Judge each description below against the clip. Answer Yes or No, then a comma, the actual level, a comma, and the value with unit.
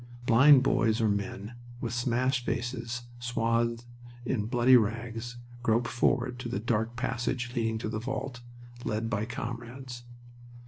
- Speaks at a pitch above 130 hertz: No, low, 120 Hz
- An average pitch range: No, narrow, 1.4 semitones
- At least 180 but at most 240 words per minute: No, slow, 135 wpm